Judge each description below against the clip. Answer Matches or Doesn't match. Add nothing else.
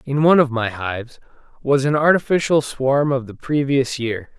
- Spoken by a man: Matches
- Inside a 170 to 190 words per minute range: Matches